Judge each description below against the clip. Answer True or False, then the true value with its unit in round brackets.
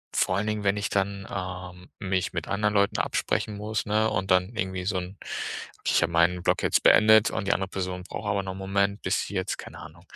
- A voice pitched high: False (95 Hz)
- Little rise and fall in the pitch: True (2.0 semitones)